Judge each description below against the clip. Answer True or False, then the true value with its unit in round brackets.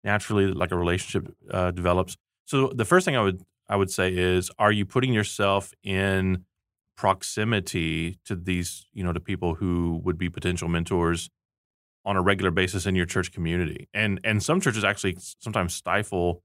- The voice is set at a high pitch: False (95 Hz)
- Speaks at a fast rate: False (175 wpm)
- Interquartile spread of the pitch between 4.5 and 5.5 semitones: False (2.4 semitones)